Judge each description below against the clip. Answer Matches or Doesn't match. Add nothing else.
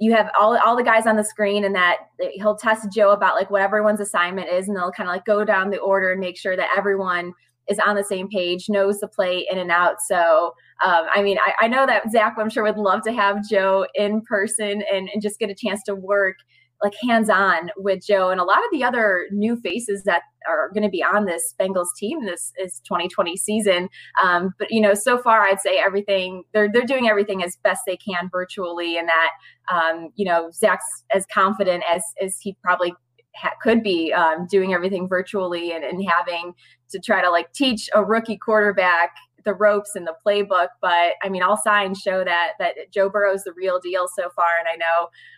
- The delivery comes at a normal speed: Doesn't match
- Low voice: Doesn't match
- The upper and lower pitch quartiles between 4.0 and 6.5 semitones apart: Doesn't match